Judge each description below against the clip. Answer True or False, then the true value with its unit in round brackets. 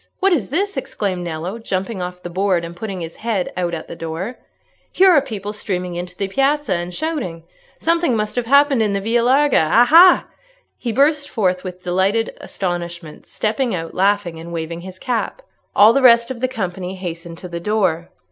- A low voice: False (195 Hz)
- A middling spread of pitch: False (5.8 semitones)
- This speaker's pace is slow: False (190 wpm)